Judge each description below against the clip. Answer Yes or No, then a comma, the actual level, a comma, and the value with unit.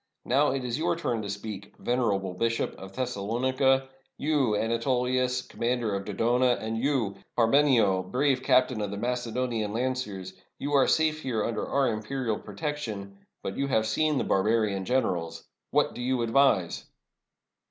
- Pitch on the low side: Yes, low, 120 Hz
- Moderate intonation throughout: Yes, average, 3.8 semitones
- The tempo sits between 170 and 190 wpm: No, average, 155 wpm